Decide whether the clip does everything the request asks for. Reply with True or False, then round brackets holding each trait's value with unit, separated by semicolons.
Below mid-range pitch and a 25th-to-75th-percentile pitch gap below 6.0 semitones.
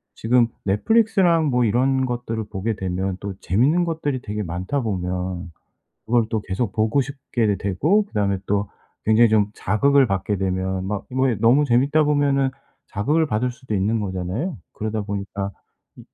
True (110 Hz; 5.5 semitones)